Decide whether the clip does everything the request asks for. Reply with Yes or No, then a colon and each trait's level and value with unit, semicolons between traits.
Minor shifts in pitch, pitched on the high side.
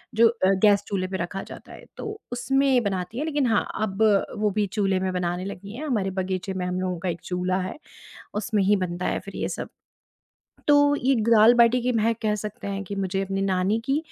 No: average, 3.7 semitones; high, 200 Hz